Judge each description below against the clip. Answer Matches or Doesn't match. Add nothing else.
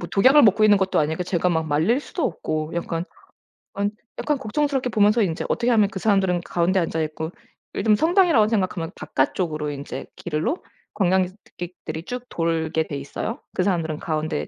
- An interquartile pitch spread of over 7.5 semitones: Doesn't match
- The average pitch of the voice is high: Doesn't match